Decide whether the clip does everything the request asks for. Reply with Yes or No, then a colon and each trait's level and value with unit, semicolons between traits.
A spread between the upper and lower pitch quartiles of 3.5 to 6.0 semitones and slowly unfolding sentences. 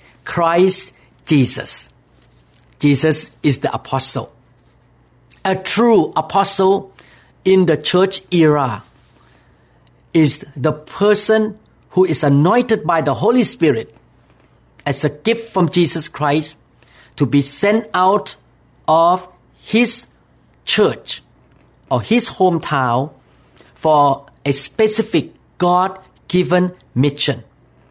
Yes: wide, 5.6 semitones; slow, 95 wpm